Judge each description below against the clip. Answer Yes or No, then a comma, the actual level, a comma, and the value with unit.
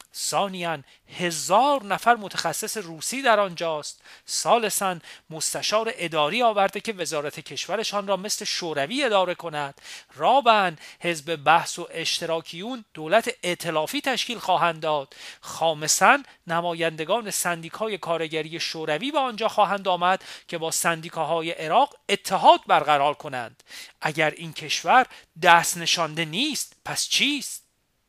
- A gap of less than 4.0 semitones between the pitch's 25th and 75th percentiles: No, average, 4.6 semitones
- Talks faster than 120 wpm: No, average, 115 wpm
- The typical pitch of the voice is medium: Yes, medium, 170 Hz